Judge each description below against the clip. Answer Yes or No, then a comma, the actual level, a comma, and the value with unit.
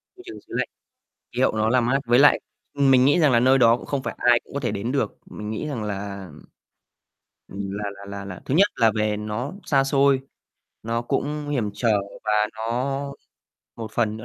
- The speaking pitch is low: Yes, low, 120 Hz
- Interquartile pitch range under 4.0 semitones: No, average, 4.3 semitones